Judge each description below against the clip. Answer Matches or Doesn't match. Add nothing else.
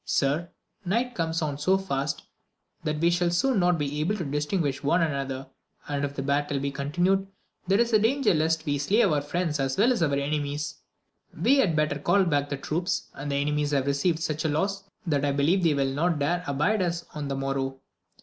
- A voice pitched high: Doesn't match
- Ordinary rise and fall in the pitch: Matches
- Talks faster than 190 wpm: Matches